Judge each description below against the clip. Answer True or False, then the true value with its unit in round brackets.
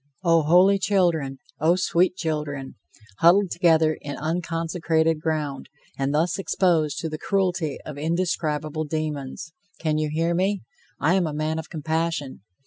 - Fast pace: False (140 wpm)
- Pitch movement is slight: True (2.2 semitones)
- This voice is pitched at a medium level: True (160 Hz)